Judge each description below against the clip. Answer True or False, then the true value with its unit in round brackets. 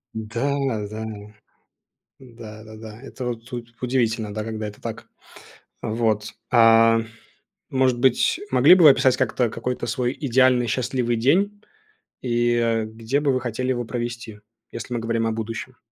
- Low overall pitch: True (120 Hz)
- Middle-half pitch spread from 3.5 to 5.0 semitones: False (2.4 semitones)